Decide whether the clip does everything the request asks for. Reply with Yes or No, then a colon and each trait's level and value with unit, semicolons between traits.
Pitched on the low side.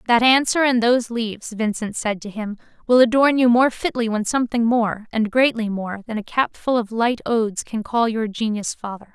No: high, 230 Hz